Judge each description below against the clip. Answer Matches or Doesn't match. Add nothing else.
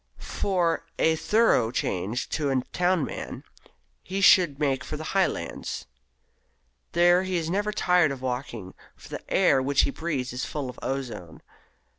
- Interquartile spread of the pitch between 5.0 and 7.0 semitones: Matches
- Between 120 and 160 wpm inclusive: Matches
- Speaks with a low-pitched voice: Doesn't match